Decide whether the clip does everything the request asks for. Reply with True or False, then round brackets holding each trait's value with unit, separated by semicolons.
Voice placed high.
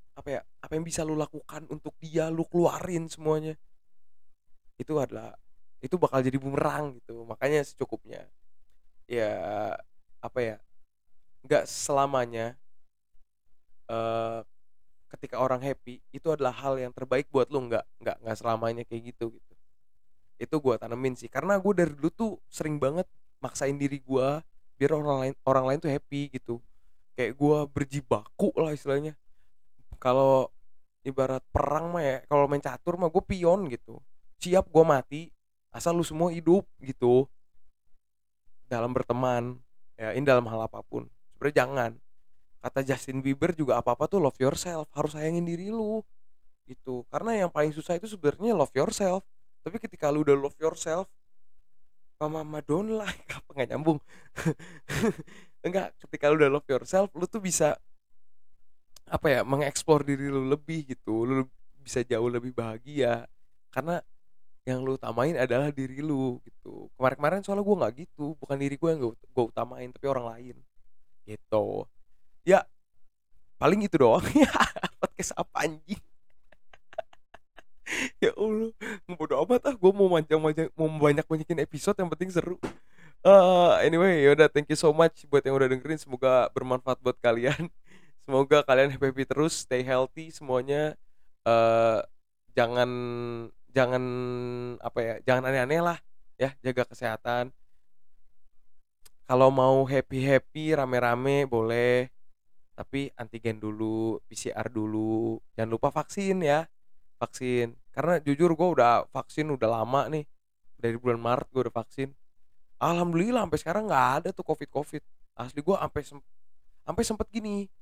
False (135 Hz)